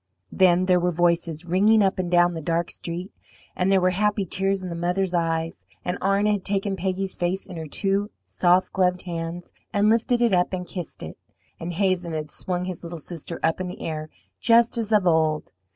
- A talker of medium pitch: Yes, medium, 180 Hz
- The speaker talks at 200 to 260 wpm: Yes, fast, 205 wpm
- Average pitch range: No, narrow, 2.3 semitones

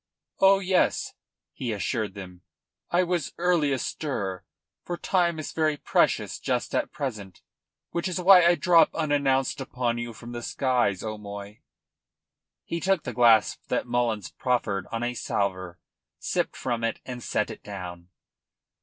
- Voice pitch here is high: No, low, 125 Hz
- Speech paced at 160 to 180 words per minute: No, average, 145 wpm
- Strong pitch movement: Yes, wide, 7.5 semitones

